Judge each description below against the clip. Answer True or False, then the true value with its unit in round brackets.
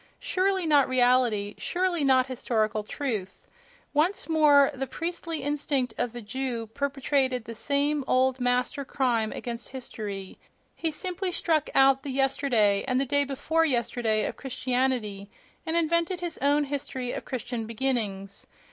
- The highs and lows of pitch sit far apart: False (3.5 semitones)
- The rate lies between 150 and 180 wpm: False (140 wpm)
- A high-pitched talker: True (265 Hz)